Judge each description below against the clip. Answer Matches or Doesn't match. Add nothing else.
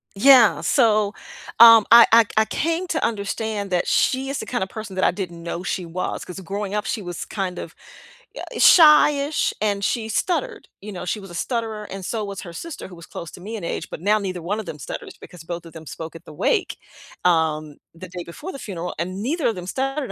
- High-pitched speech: Matches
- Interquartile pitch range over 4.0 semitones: Matches